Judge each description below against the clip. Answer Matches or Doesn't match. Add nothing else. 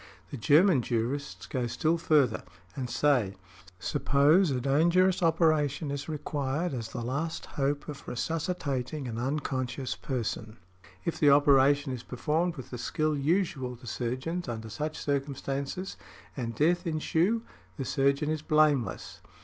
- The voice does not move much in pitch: Doesn't match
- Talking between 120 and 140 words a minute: Matches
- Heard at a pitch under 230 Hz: Matches